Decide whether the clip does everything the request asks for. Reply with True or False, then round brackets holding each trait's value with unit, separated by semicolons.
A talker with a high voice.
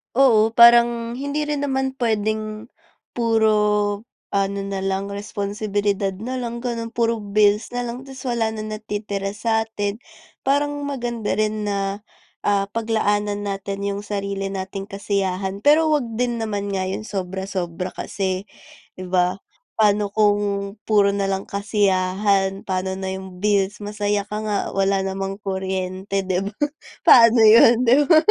True (205 Hz)